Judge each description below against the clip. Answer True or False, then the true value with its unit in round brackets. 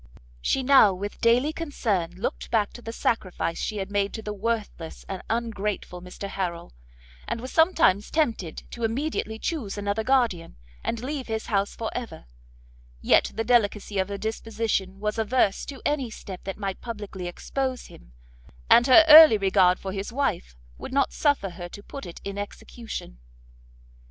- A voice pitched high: True (215 Hz)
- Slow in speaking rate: False (165 wpm)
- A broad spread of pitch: False (3.9 semitones)